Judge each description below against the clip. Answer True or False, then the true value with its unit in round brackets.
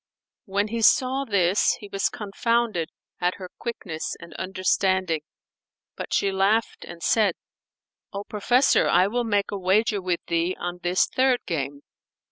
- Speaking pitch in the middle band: False (195 Hz)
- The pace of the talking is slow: False (145 wpm)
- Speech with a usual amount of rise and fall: True (3.6 semitones)